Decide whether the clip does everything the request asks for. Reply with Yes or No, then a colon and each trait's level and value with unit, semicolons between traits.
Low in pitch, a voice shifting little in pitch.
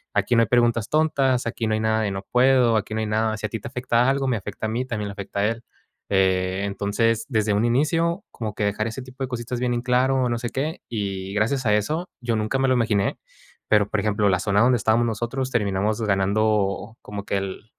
No: low, 110 Hz; average, 3.2 semitones